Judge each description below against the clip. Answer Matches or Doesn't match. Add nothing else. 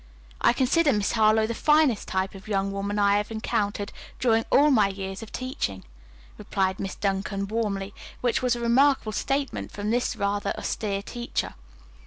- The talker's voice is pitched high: Matches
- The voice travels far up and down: Doesn't match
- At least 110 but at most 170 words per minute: Matches